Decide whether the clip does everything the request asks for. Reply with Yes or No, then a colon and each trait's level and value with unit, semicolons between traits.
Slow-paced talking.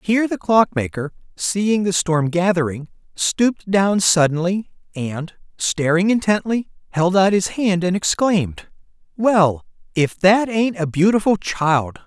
Yes: slow, 130 wpm